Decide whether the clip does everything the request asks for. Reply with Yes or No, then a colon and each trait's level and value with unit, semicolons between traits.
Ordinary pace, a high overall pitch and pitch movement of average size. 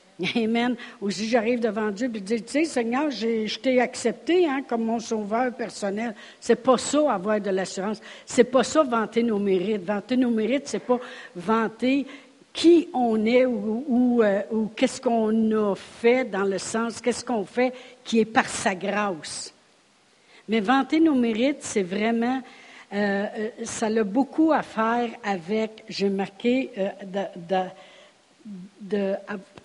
Yes: average, 170 wpm; high, 230 Hz; average, 3.3 semitones